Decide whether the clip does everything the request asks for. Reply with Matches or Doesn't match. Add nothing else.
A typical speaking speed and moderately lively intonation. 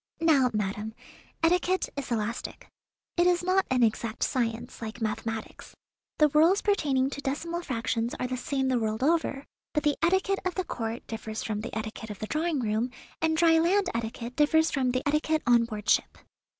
Doesn't match